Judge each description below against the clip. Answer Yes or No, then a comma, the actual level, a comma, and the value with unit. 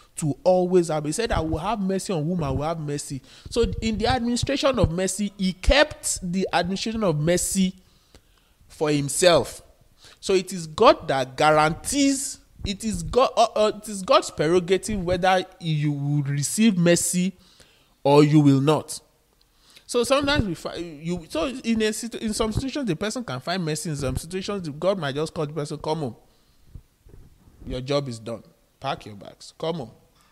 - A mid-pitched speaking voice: Yes, medium, 175 Hz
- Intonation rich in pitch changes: Yes, wide, 6.0 semitones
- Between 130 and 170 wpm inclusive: No, average, 180 wpm